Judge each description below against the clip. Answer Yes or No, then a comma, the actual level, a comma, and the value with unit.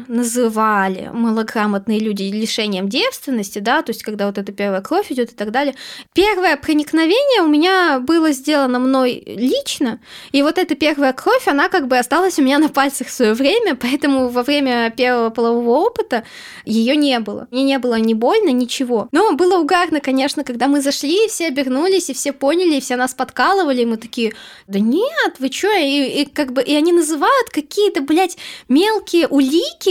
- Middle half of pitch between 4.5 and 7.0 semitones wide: Yes, average, 5.2 semitones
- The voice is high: Yes, very high, 275 Hz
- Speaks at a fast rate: Yes, fast, 185 wpm